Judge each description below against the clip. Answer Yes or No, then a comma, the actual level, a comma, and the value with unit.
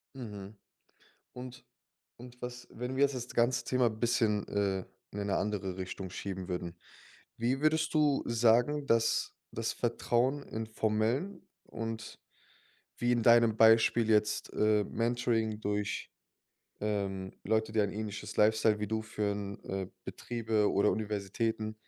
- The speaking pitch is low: Yes, low, 110 Hz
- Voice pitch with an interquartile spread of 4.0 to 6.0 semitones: No, average, 2.7 semitones